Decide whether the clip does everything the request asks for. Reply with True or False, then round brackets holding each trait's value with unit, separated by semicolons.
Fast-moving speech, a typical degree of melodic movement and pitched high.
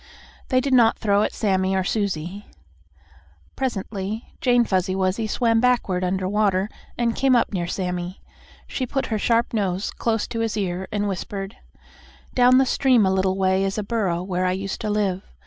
False (175 wpm; 3.4 semitones; 200 Hz)